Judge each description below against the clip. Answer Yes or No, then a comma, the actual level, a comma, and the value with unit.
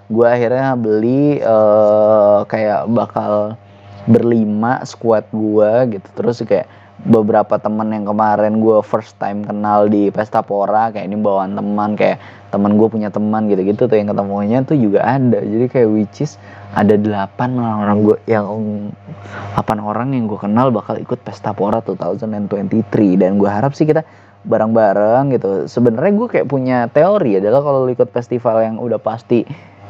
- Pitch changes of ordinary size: No, narrow, 2.2 semitones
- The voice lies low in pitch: Yes, low, 110 Hz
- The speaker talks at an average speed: No, fast, 160 wpm